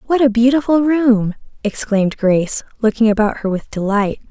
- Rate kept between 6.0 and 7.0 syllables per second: No, 5.3 syllables/s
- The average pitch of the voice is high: Yes, high, 230 Hz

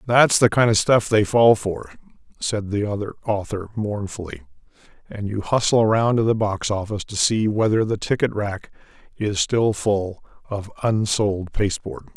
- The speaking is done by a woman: No, male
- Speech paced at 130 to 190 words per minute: Yes, average, 165 wpm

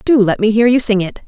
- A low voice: No, high, 220 Hz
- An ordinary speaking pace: No, fast, 330 wpm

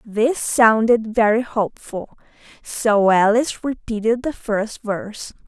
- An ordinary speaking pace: No, slow, 110 wpm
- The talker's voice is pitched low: No, high, 225 Hz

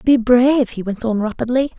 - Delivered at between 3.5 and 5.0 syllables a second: No, 5.2 syllables/s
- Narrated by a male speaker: No, female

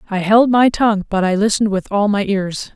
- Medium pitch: No, high, 205 Hz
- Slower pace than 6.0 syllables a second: Yes, 5.7 syllables/s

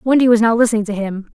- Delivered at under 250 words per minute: No, fast, 265 wpm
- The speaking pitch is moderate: No, high, 225 Hz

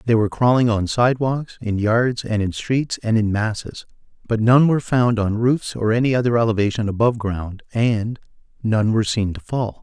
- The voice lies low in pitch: Yes, low, 115 Hz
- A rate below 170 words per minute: No, average, 185 wpm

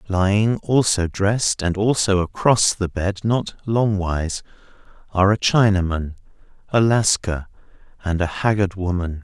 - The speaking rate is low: Yes, slow, 125 wpm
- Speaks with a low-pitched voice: Yes, low, 100 Hz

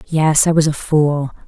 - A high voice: No, medium, 150 Hz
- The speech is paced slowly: No, fast, 205 wpm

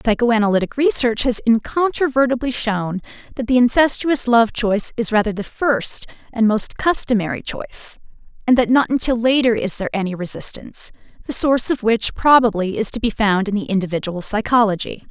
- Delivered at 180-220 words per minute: No, average, 160 wpm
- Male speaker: No, female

